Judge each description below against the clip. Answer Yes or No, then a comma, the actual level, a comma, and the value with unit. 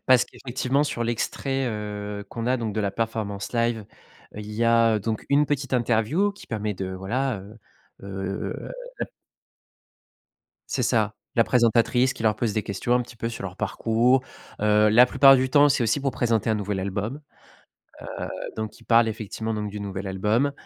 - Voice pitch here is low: Yes, low, 115 Hz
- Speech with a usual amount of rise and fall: Yes, average, 3.1 semitones